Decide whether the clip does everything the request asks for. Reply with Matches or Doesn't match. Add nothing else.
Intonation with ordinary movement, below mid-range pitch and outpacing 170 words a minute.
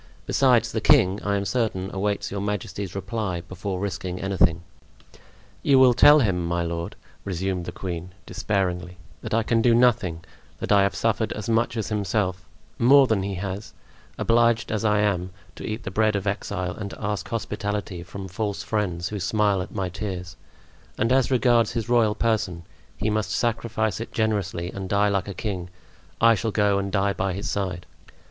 Matches